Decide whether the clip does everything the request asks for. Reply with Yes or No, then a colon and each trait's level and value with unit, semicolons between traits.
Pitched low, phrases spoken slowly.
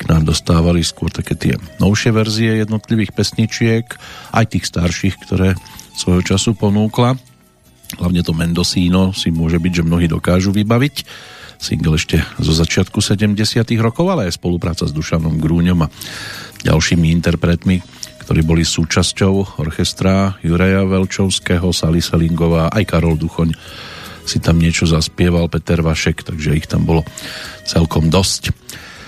No: very low, 90 Hz; average, 130 wpm